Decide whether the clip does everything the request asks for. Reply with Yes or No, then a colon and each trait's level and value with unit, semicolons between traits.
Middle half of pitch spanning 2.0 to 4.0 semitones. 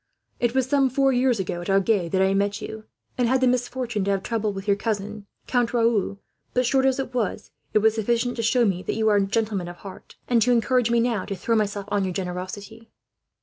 Yes: average, 3.6 semitones